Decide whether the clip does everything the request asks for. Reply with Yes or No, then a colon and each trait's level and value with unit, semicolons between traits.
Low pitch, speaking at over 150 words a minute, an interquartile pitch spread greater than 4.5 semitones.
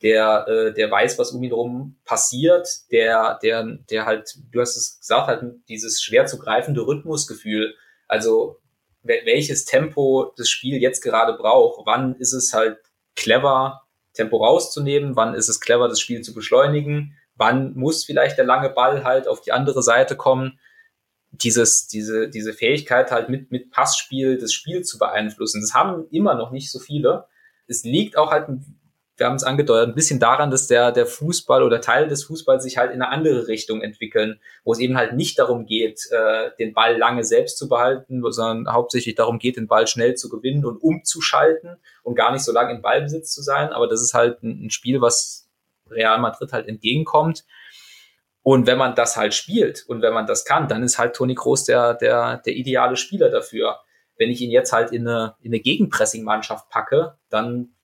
Yes: low, 125 Hz; fast, 190 wpm; average, 4.9 semitones